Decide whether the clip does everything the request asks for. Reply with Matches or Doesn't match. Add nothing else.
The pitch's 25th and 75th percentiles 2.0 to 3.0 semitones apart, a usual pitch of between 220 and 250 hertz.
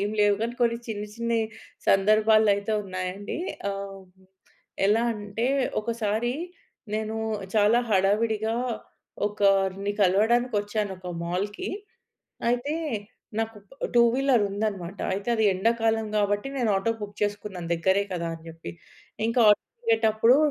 Doesn't match